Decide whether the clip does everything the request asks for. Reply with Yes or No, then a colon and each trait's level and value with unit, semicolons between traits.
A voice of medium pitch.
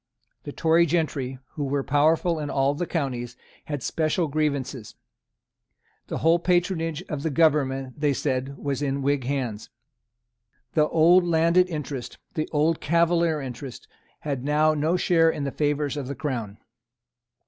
Yes: medium, 150 Hz